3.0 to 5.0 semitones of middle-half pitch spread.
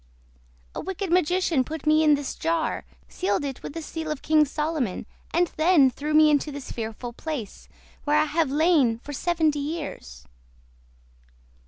No: narrow, 2.6 semitones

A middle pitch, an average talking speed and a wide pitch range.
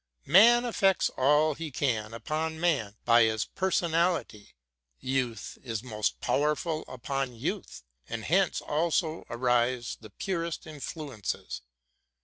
No: medium, 145 Hz; slow, 120 wpm; wide, 5.9 semitones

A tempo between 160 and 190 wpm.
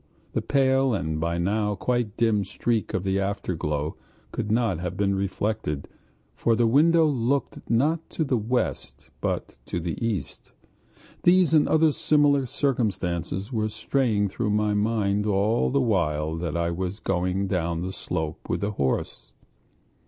No: average, 150 wpm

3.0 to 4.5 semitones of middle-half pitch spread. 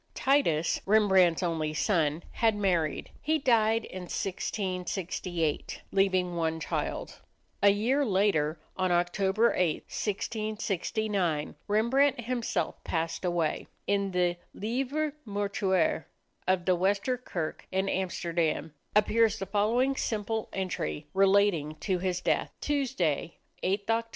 Yes: average, 3.9 semitones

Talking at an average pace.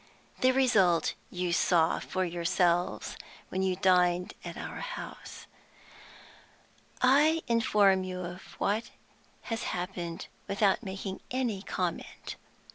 No: slow, 110 wpm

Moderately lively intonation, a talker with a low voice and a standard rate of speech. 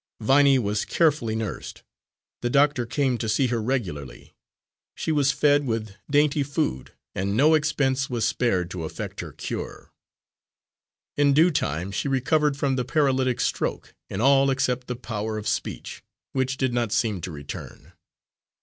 Yes: average, 4.5 semitones; low, 130 Hz; average, 155 wpm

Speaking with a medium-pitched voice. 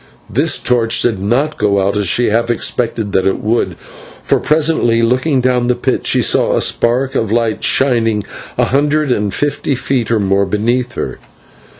No: low, 120 Hz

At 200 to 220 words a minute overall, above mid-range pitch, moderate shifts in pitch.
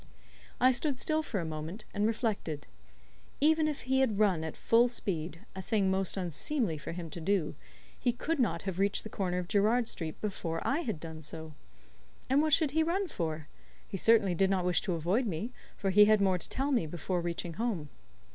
No: fast, 205 wpm; high, 195 Hz; wide, 6.2 semitones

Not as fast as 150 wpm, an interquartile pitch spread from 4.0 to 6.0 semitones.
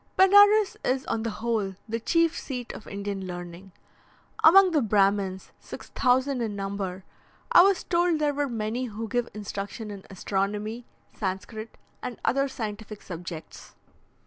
Yes: average, 140 wpm; average, 5.3 semitones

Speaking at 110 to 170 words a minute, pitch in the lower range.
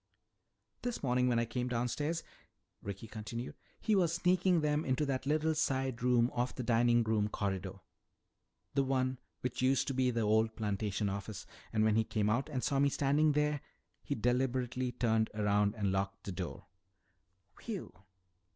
Yes: average, 165 wpm; low, 125 Hz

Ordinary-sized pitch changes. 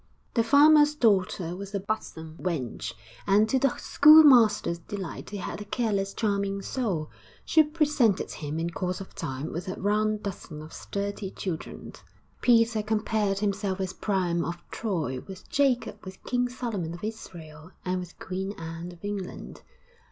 Yes: average, 4.1 semitones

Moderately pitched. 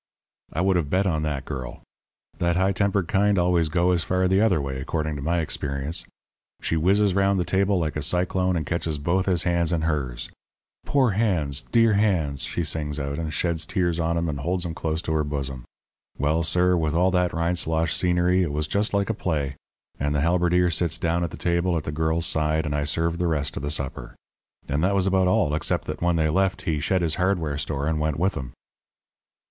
No: very low, 85 Hz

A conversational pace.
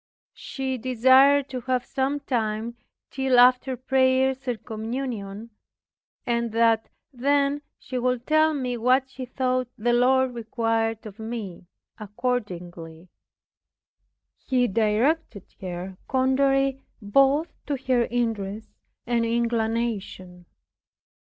No: slow, 105 wpm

